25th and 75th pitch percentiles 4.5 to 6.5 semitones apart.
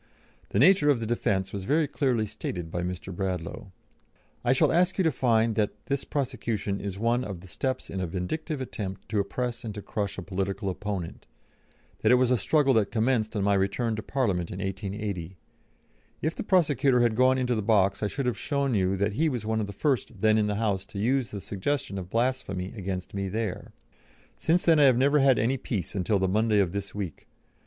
Yes: average, 4.8 semitones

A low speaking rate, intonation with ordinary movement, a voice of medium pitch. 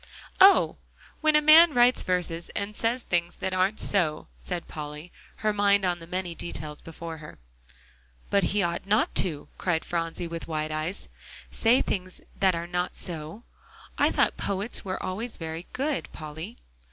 No: average, 165 wpm; average, 4.0 semitones; medium, 180 Hz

